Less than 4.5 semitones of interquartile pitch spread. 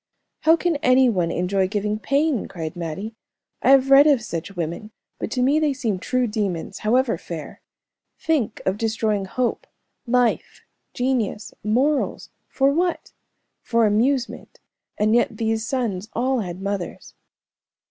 No: average, 4.9 semitones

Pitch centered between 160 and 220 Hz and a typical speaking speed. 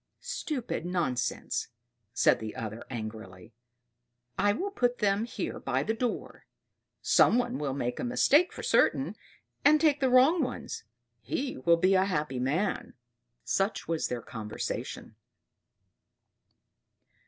No: high, 190 Hz; slow, 130 wpm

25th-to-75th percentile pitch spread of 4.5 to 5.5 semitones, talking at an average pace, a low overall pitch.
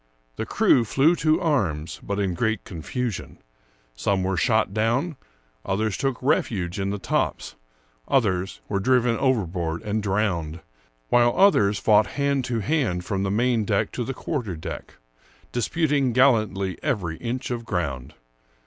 Yes: average, 5.0 semitones; average, 145 wpm; low, 110 Hz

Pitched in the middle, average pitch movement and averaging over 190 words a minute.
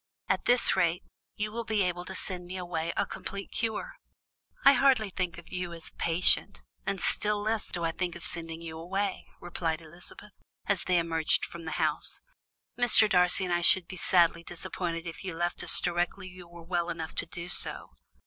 No: medium, 175 Hz; narrow, 2.3 semitones; fast, 205 wpm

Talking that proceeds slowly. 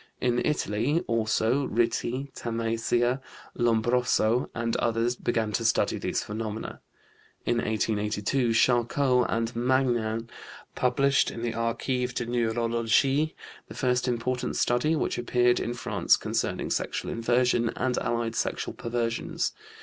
Yes: slow, 120 wpm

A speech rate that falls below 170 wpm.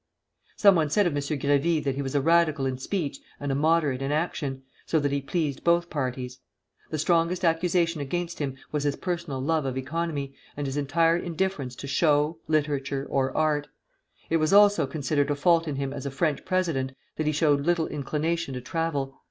No: average, 195 wpm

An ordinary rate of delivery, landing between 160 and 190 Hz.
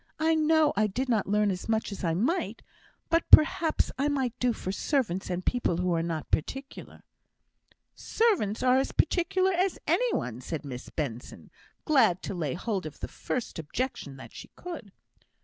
No: average, 175 wpm; high, 220 Hz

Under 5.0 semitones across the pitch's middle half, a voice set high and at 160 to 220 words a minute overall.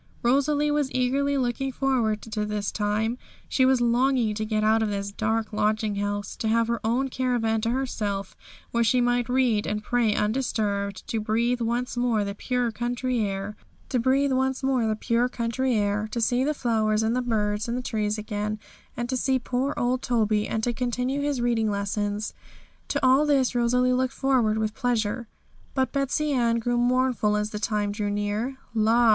Yes: average, 3.0 semitones; high, 235 Hz; average, 175 wpm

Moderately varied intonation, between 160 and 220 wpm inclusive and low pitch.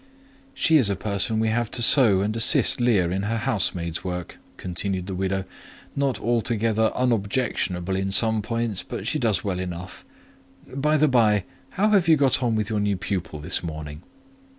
Yes: average, 4.2 semitones; average, 175 wpm; low, 105 Hz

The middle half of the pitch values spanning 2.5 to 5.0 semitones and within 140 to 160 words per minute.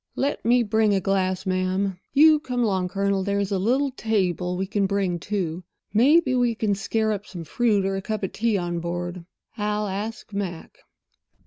No: average, 3.0 semitones; average, 180 wpm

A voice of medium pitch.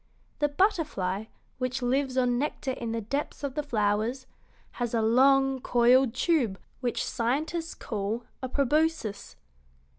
No: very high, 255 Hz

